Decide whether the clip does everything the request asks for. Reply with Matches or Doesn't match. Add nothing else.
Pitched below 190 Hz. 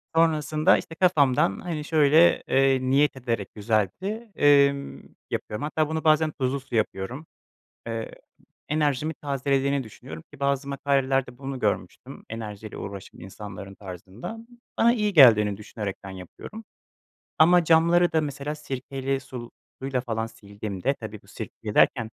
Matches